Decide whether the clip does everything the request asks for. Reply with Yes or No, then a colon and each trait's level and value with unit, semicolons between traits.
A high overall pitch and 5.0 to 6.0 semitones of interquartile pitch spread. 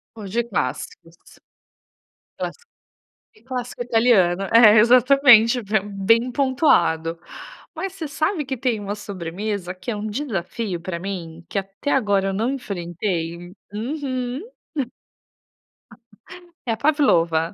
Yes: high, 215 Hz; wide, 5.6 semitones